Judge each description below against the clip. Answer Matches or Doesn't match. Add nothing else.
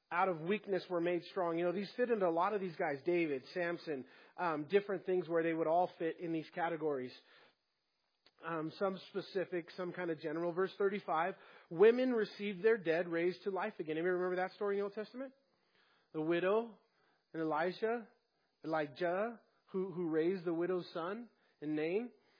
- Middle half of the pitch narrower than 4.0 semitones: Matches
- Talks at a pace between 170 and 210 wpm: Matches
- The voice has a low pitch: Doesn't match